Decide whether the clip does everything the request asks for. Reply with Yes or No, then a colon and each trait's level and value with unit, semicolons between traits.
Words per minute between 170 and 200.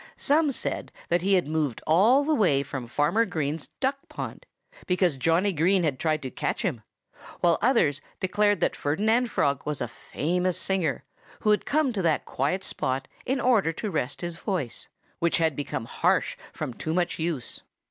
Yes: average, 180 wpm